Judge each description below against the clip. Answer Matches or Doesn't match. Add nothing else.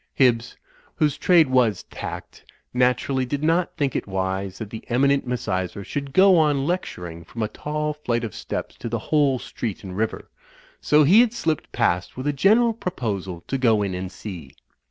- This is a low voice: Matches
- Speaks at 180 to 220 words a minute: Matches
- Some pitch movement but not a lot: Doesn't match